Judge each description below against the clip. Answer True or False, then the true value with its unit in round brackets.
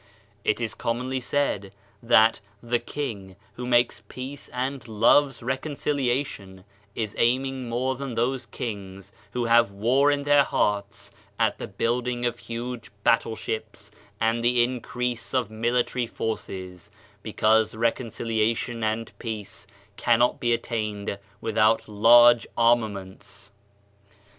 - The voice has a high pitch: False (115 Hz)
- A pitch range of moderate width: False (2.3 semitones)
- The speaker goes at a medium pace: False (120 wpm)